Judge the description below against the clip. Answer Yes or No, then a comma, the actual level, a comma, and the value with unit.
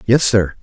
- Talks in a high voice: No, low, 105 Hz